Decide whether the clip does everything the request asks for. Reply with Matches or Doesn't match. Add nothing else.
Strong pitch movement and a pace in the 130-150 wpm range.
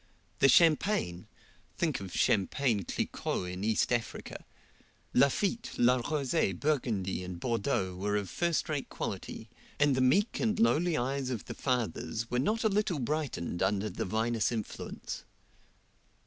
Matches